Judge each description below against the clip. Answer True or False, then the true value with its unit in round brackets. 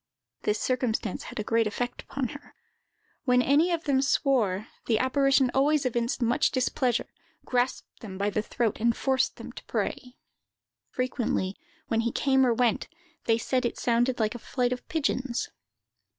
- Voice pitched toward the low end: False (250 Hz)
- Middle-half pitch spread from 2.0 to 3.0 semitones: True (2.6 semitones)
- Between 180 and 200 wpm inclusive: False (165 wpm)